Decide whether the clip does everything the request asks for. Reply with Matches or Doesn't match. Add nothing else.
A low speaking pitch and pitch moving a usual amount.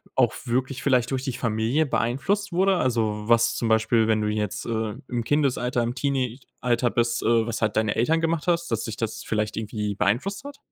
Matches